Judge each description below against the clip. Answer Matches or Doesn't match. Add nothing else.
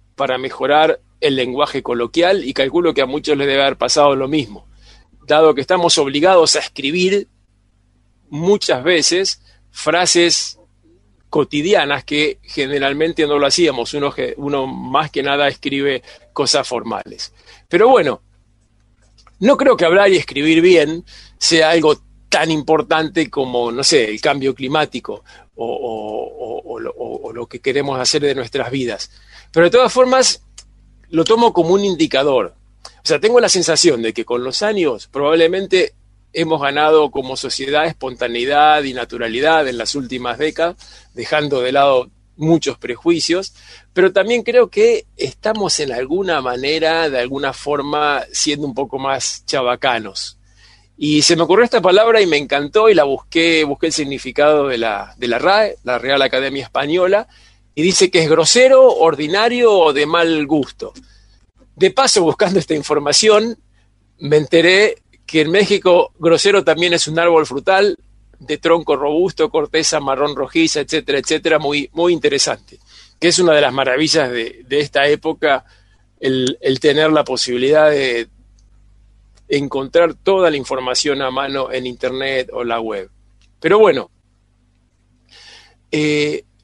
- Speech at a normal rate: Matches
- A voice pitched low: Doesn't match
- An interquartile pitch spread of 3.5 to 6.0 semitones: Matches